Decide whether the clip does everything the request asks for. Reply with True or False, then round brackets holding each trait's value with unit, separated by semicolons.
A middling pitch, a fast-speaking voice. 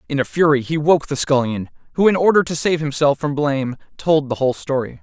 True (145 Hz; 225 wpm)